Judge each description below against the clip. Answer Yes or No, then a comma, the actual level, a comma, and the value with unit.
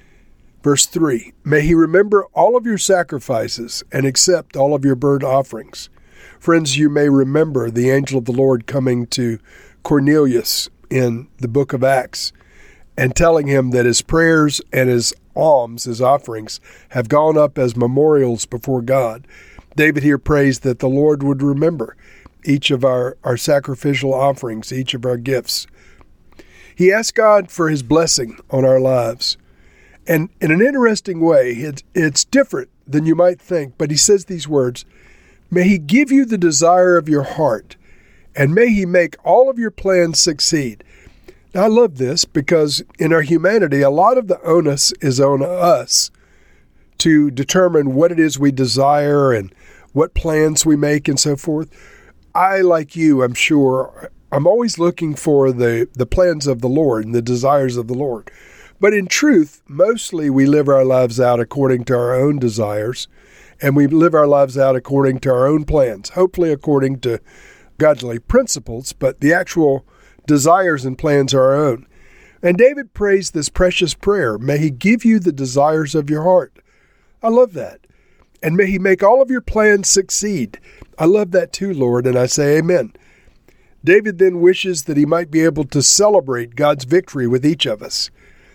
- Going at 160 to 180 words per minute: Yes, average, 175 wpm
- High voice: No, medium, 145 Hz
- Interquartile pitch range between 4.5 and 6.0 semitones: Yes, average, 4.8 semitones